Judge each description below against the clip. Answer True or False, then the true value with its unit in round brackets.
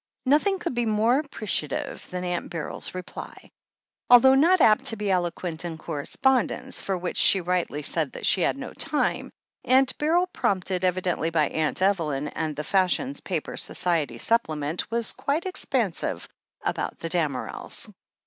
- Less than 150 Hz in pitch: False (185 Hz)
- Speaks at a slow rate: False (150 wpm)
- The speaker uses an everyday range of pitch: False (7.7 semitones)